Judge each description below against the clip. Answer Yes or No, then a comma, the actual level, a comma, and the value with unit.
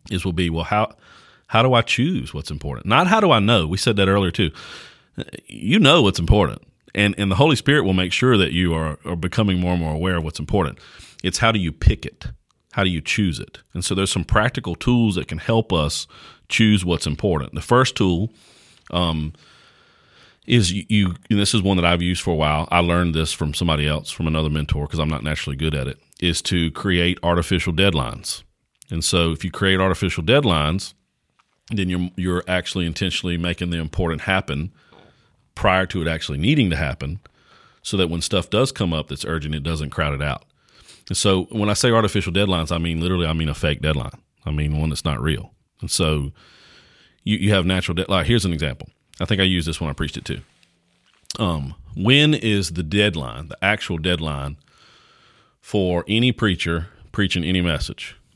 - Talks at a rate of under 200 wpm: No, fast, 205 wpm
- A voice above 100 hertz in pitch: No, very low, 90 Hz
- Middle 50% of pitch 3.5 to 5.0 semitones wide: Yes, average, 4.0 semitones